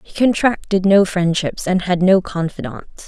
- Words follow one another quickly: No, average, 155 wpm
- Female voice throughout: Yes, female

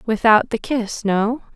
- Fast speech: No, average, 155 wpm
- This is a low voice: No, high, 220 Hz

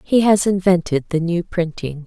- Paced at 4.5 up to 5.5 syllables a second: Yes, 4.6 syllables/s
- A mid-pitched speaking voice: Yes, medium, 175 Hz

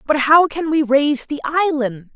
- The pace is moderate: Yes, average, 195 wpm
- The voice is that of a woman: Yes, female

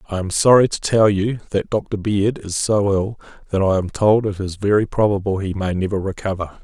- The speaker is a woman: No, male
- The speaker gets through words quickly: Yes, fast, 215 wpm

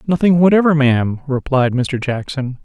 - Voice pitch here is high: No, medium, 140 Hz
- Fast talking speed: No, slow, 135 wpm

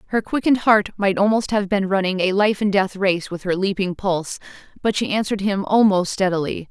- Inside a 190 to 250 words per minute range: Yes, fast, 205 wpm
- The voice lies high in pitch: Yes, high, 195 Hz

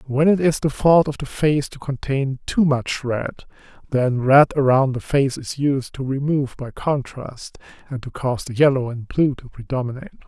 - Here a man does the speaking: Yes, male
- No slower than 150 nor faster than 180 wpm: No, average, 195 wpm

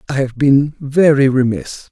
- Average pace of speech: Yes, average, 155 wpm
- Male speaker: Yes, male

